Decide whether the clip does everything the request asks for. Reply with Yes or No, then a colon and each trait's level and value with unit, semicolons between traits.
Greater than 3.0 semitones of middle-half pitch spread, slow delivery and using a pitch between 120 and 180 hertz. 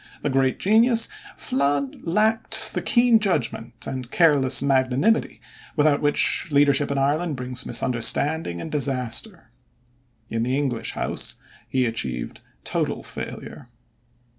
Yes: average, 4.0 semitones; slow, 115 wpm; medium, 140 Hz